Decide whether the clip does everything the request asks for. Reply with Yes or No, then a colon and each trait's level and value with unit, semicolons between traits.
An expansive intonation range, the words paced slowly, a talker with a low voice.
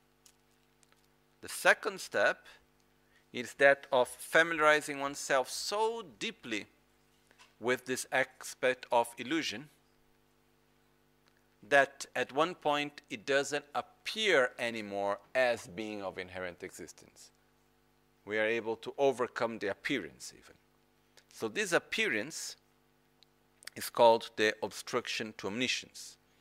Yes: wide, 5.7 semitones; slow, 100 wpm; low, 120 Hz